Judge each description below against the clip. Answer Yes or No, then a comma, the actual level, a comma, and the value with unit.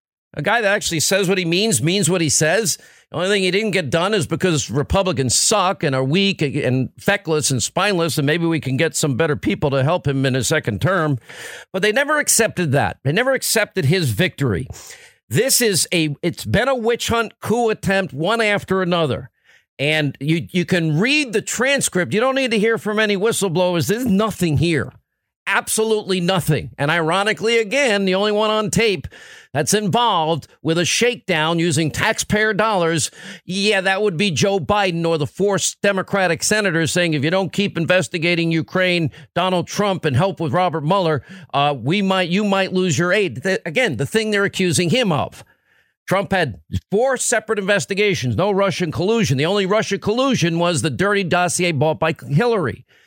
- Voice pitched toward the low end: No, medium, 180 Hz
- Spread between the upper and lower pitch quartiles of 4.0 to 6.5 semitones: Yes, average, 4.5 semitones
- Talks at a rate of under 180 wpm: No, average, 185 wpm